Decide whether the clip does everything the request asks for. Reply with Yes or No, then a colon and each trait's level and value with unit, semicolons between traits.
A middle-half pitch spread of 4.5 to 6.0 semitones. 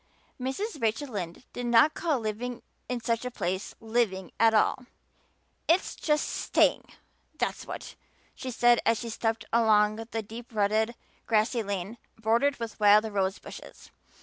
No: narrow, 2.4 semitones